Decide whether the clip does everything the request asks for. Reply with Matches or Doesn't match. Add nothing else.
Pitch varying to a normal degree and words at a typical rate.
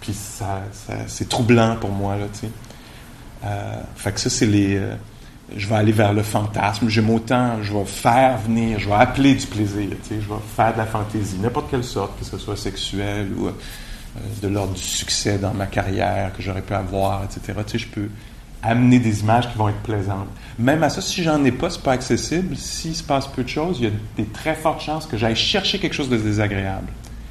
Doesn't match